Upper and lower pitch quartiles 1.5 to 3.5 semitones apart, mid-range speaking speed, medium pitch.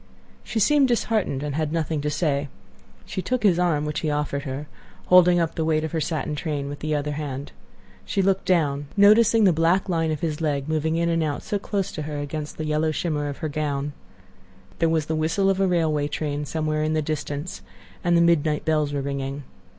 No: narrow, 2.6 semitones; fast, 215 wpm; medium, 155 Hz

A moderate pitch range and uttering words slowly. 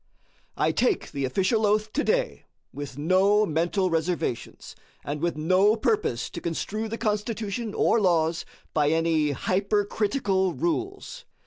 Yes: average, 5.0 semitones; slow, 125 wpm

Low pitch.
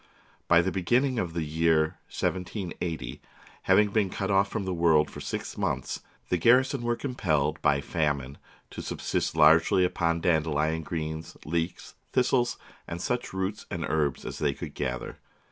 Yes: very low, 85 Hz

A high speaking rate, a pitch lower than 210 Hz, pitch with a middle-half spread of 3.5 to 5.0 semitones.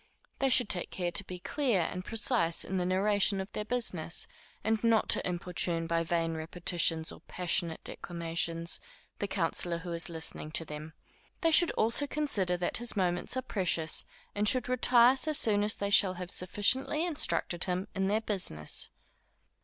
No: average, 170 wpm; medium, 185 Hz; average, 4.6 semitones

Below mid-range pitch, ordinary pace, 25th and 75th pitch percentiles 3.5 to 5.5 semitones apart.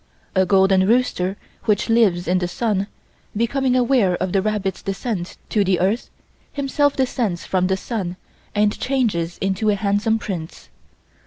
No: high, 200 Hz; average, 150 wpm; average, 3.8 semitones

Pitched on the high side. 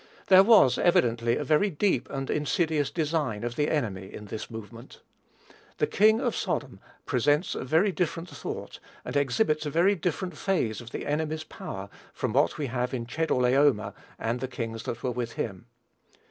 No: medium, 140 Hz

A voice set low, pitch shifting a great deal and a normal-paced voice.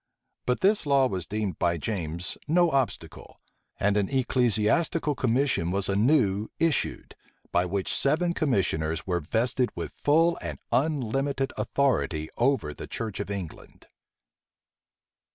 No: low, 115 Hz; wide, 6.6 semitones; slow, 125 wpm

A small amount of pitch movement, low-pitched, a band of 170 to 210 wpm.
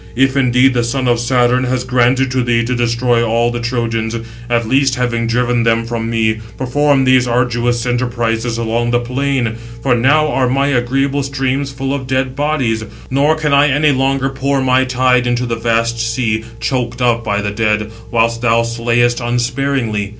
Yes: narrow, 2.2 semitones; low, 120 Hz; average, 180 wpm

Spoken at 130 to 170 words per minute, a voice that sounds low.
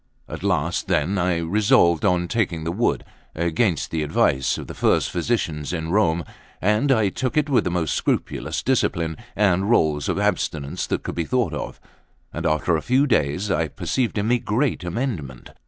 No: average, 185 wpm; very low, 90 Hz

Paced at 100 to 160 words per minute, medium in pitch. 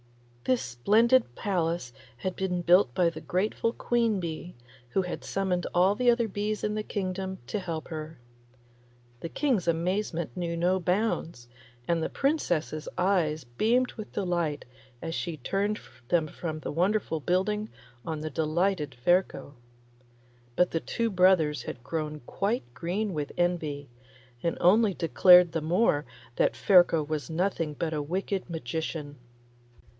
Yes: average, 145 wpm; medium, 175 Hz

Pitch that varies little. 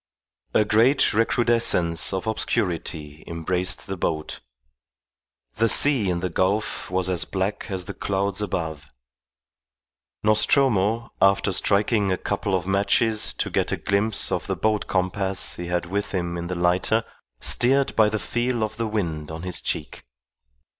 No: average, 3.4 semitones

